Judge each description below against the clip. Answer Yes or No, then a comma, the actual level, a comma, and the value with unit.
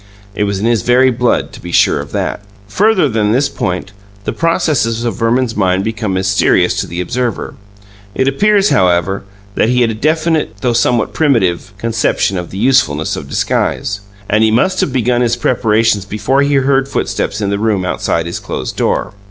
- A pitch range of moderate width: Yes, average, 4.7 semitones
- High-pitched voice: No, low, 115 Hz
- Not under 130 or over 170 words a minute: No, average, 185 wpm